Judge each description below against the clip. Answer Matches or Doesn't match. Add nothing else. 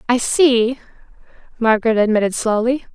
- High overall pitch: Matches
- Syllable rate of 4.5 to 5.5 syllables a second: Matches